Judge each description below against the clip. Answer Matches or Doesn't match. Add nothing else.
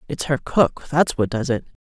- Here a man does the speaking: Doesn't match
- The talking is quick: Matches